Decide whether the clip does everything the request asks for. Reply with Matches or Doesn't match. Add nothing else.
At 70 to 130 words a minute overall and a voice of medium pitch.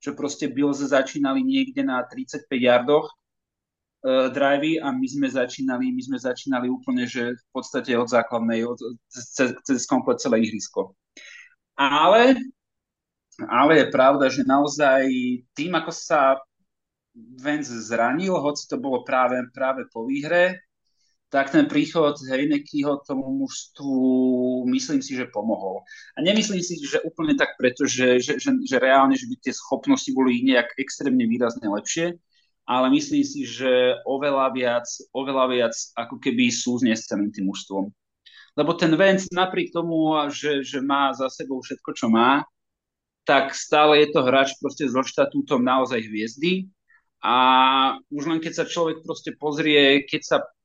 Doesn't match